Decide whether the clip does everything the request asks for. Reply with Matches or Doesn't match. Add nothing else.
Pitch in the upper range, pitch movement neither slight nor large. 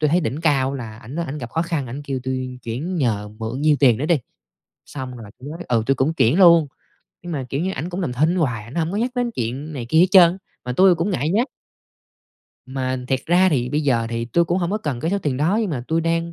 Doesn't match